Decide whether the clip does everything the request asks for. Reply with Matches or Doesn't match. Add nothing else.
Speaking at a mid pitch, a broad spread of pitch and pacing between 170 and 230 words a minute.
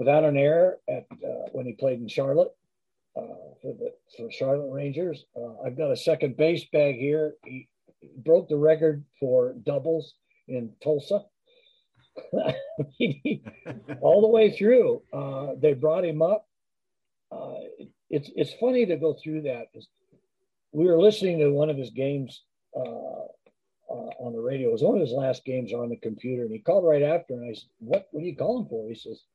Matches